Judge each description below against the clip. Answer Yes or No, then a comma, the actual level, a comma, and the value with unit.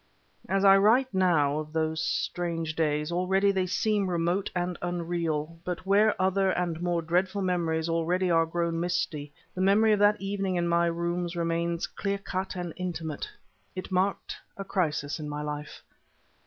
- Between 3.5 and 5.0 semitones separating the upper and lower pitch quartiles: No, narrow, 2.5 semitones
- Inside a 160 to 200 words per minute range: Yes, average, 165 wpm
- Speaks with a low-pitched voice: No, medium, 175 Hz